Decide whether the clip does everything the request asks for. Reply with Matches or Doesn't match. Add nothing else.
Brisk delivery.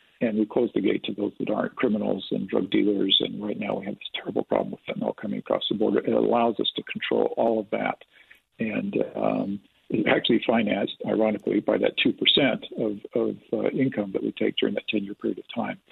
Matches